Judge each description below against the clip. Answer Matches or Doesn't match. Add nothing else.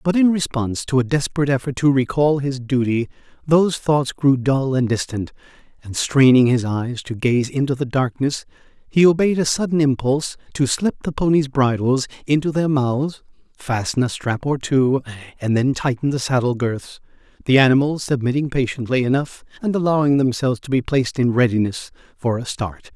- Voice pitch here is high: Doesn't match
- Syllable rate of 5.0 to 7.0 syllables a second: Matches